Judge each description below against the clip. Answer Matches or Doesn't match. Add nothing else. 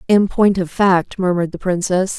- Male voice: Doesn't match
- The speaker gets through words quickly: Doesn't match